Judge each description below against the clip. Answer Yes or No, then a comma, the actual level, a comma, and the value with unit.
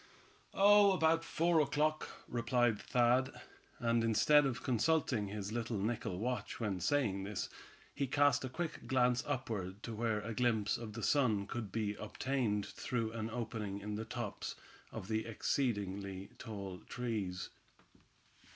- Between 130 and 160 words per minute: Yes, average, 140 wpm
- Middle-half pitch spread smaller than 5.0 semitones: Yes, average, 3.9 semitones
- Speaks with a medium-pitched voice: No, low, 115 Hz